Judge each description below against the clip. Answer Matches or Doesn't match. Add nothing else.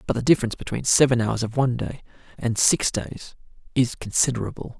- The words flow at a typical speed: Matches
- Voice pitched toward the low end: Matches